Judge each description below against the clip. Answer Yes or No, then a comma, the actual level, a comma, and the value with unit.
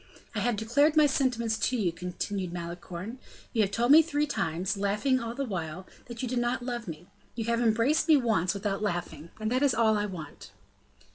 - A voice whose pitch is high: Yes, high, 220 Hz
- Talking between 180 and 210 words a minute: Yes, fast, 205 wpm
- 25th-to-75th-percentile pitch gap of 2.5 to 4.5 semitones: No, average, 5.0 semitones